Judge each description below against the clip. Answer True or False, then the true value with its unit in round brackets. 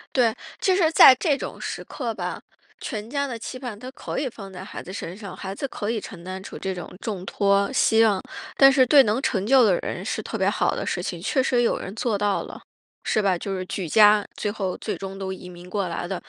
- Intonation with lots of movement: False (4.5 semitones)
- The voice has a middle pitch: False (210 Hz)